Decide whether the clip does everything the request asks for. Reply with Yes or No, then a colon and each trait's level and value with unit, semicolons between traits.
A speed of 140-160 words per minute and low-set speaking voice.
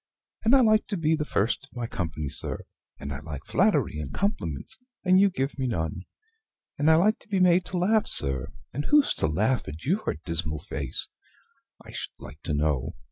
No: average, 200 wpm; low, 130 Hz